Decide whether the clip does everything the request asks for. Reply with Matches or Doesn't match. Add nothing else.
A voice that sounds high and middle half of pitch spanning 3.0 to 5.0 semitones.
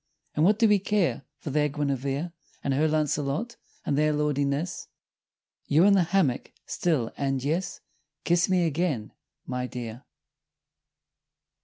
Doesn't match